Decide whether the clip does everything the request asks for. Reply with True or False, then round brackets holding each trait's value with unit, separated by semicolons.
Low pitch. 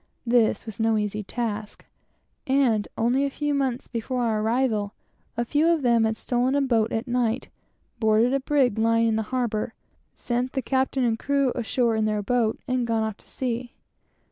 False (235 Hz)